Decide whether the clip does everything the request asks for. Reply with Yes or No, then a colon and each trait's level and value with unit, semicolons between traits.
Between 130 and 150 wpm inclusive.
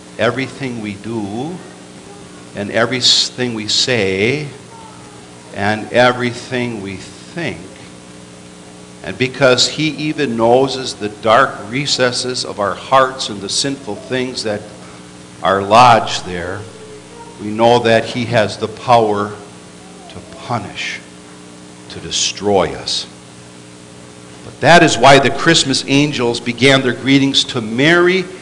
No: slow, 115 wpm